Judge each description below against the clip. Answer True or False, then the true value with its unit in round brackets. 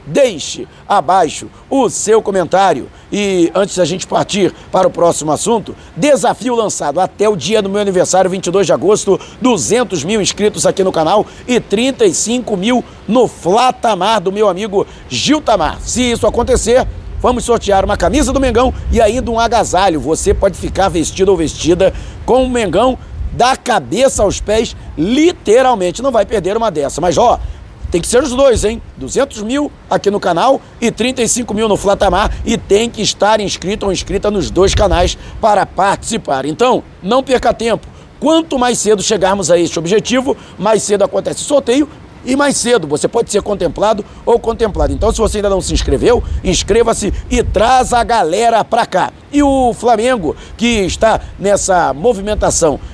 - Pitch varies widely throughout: False (4.3 semitones)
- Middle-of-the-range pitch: False (215 Hz)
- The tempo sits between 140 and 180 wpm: True (170 wpm)